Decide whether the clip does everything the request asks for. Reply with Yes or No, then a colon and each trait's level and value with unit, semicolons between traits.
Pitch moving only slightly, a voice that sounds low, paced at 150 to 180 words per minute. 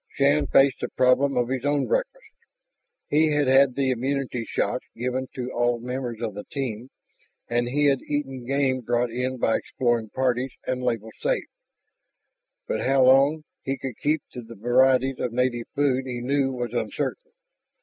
Yes: narrow, 2.2 semitones; low, 130 Hz; average, 170 wpm